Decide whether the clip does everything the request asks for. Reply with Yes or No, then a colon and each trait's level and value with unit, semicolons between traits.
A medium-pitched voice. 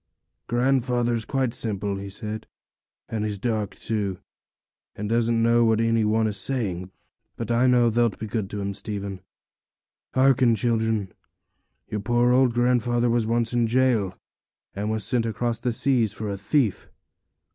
No: low, 115 Hz